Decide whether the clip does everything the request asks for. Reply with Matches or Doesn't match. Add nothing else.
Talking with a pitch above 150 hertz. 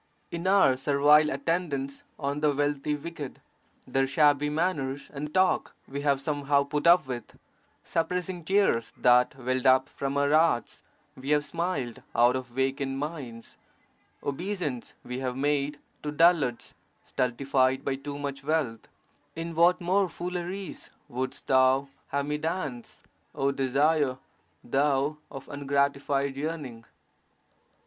Doesn't match